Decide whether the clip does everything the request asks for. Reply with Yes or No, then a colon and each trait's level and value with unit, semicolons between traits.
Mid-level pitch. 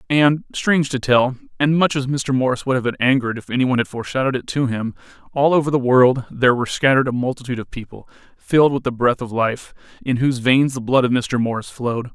No: low, 130 Hz